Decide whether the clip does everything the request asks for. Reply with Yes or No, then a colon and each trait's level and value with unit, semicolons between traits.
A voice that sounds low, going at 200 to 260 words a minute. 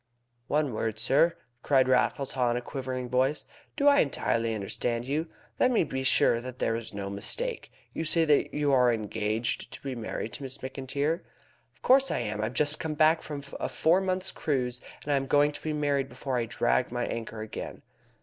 Yes: low, 130 Hz; fast, 205 wpm